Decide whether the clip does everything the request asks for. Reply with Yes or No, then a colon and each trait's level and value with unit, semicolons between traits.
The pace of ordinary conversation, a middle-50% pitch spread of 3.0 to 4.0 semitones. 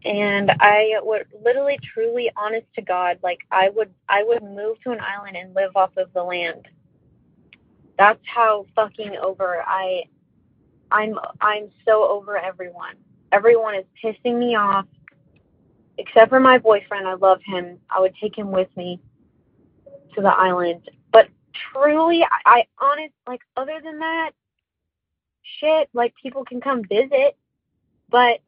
No: average, 150 wpm; average, 4.7 semitones